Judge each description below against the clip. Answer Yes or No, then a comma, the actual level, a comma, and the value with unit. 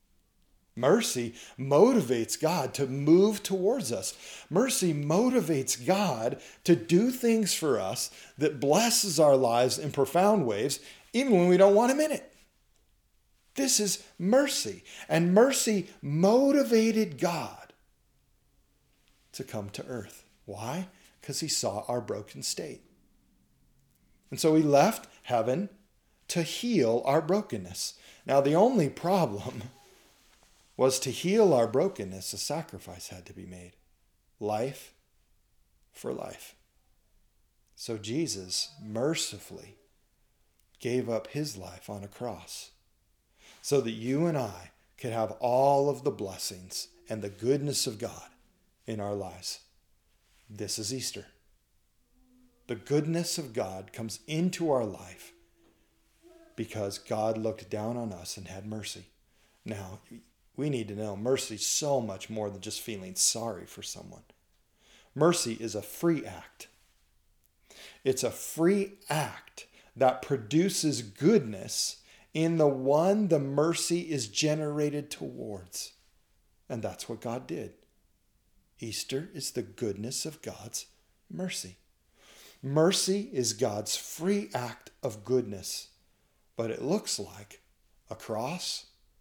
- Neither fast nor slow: No, slow, 125 wpm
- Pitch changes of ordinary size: No, wide, 8.3 semitones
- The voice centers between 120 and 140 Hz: Yes, low, 135 Hz